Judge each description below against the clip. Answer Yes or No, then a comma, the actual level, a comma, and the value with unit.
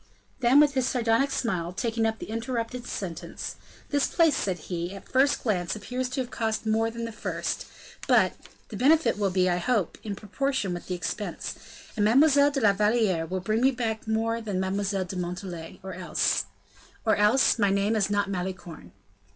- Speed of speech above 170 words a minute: Yes, average, 185 wpm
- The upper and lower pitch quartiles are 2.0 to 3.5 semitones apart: No, average, 4.5 semitones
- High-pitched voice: Yes, high, 215 Hz